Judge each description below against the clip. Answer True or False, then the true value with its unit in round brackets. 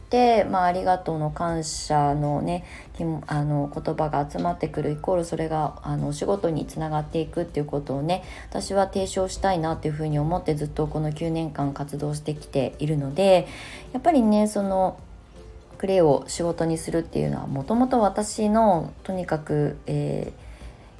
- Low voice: False (155 Hz)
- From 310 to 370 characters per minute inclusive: True (325 characters per minute)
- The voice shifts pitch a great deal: False (4.0 semitones)